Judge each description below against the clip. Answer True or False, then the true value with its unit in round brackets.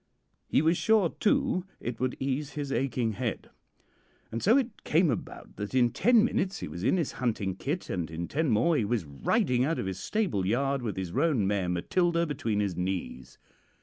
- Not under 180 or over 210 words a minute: True (195 wpm)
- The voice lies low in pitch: True (125 Hz)